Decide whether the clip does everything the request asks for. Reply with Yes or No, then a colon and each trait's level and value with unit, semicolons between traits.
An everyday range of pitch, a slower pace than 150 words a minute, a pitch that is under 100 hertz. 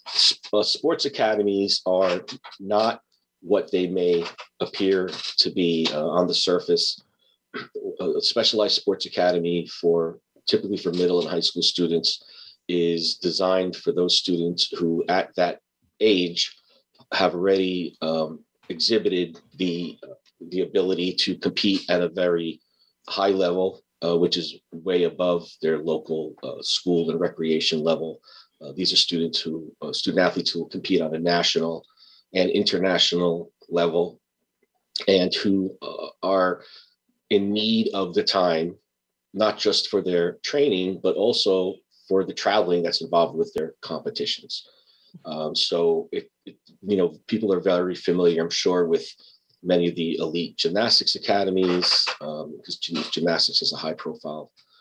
No: narrow, 2.2 semitones; average, 140 wpm; very low, 90 Hz